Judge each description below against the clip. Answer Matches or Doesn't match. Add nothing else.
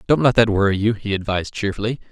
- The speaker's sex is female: Doesn't match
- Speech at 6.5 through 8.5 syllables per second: Matches